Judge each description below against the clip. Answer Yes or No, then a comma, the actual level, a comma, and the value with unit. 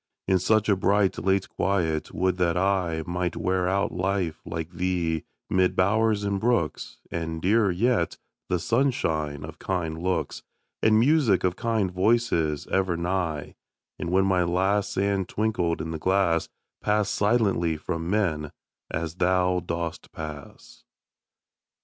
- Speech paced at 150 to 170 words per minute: No, average, 140 wpm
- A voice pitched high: No, very low, 90 Hz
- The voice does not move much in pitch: No, average, 3.1 semitones